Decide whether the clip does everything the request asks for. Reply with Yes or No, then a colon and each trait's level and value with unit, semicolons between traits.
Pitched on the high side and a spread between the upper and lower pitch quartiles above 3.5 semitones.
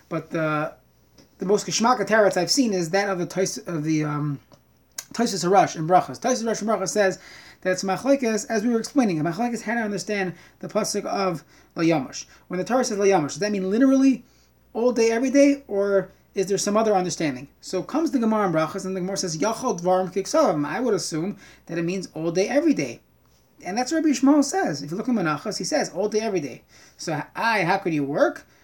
Yes: high, 195 Hz; average, 4.2 semitones